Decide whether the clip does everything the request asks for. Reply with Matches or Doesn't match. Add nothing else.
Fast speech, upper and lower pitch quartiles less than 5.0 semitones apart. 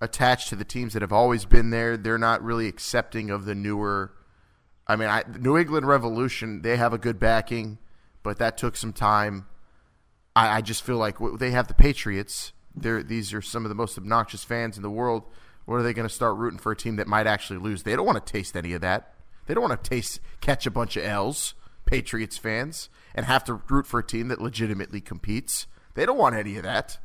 Matches